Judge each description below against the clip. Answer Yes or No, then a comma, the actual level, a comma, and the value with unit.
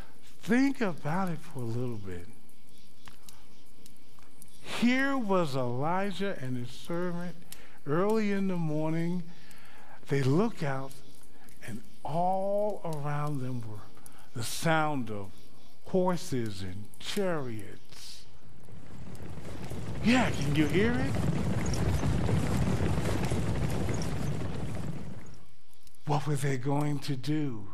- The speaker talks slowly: Yes, slow, 90 wpm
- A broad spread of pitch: Yes, wide, 6.2 semitones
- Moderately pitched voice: Yes, medium, 150 Hz